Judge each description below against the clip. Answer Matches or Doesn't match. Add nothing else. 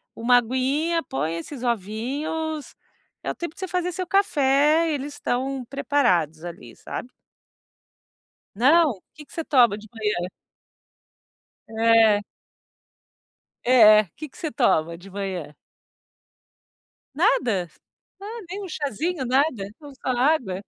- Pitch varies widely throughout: Matches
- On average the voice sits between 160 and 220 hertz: Doesn't match